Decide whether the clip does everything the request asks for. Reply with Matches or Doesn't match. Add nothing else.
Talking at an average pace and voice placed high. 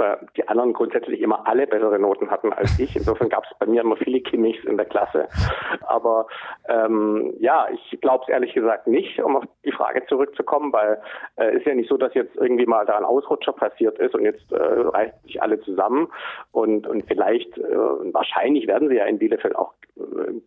Doesn't match